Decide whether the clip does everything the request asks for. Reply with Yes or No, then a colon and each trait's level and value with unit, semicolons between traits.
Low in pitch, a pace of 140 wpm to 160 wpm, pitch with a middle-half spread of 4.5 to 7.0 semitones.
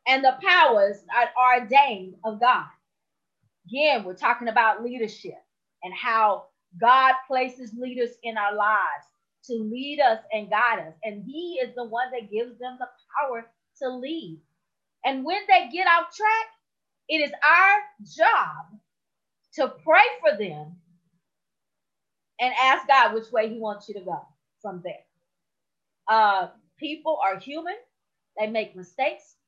No: high, 240 Hz; average, 145 wpm; average, 5.1 semitones